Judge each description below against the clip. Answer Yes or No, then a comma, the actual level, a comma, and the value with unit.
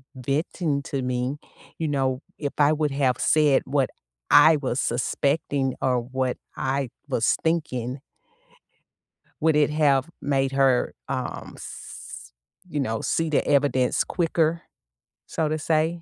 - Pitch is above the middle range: No, medium, 140 Hz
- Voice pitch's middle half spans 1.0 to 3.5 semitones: Yes, average, 2.8 semitones